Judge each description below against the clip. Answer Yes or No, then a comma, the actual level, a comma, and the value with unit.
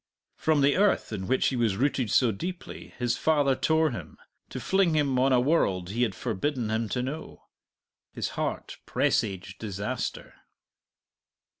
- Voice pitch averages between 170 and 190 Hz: No, low, 125 Hz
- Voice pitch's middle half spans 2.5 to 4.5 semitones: No, average, 5.3 semitones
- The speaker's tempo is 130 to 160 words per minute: Yes, average, 155 wpm